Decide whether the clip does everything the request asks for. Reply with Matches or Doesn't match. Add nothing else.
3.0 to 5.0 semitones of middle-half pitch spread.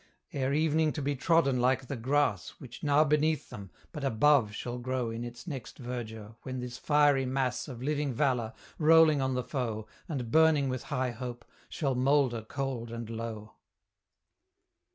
Matches